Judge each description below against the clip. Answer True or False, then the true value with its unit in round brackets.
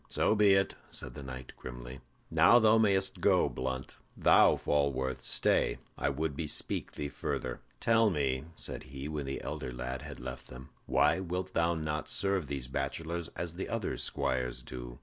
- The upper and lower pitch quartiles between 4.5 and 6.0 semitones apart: True (5.4 semitones)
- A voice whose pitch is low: True (70 Hz)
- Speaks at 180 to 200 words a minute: False (170 wpm)